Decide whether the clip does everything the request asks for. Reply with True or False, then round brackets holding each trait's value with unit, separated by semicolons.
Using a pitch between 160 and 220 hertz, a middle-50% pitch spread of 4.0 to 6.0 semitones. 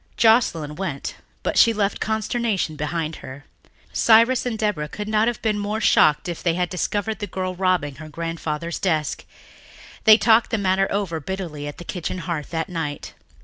True (185 Hz; 5.1 semitones)